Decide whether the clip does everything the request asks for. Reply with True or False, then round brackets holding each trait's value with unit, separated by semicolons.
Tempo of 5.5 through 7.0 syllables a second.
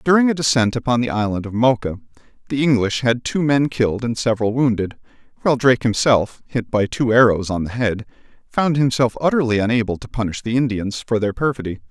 True (6.0 syllables/s)